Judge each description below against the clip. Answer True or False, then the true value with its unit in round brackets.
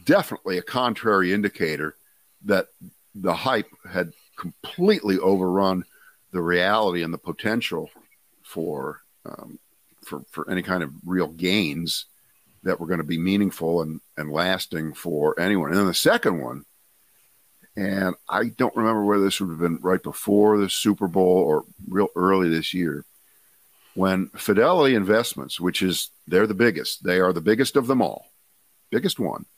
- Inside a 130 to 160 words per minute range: True (155 wpm)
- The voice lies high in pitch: False (95 Hz)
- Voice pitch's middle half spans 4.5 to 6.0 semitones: False (3.0 semitones)